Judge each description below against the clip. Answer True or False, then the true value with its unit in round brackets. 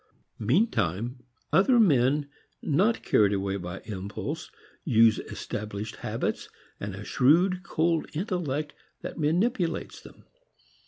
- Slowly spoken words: True (105 wpm)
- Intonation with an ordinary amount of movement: False (8.8 semitones)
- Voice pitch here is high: False (140 Hz)